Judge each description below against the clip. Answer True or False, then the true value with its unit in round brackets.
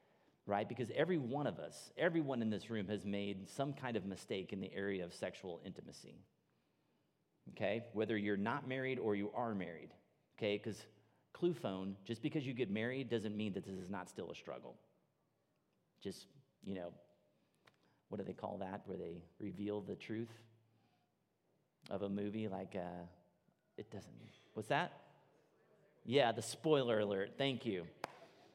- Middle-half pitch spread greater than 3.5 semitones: False (3.2 semitones)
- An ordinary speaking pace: True (160 wpm)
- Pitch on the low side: True (105 Hz)